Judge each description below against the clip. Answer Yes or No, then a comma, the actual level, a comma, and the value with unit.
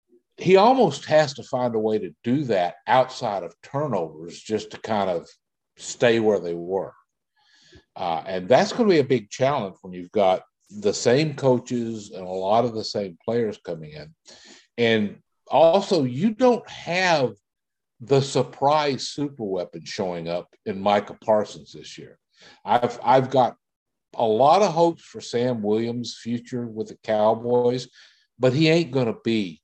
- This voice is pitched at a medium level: No, low, 120 Hz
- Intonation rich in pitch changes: Yes, wide, 6.0 semitones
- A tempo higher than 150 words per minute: Yes, average, 165 wpm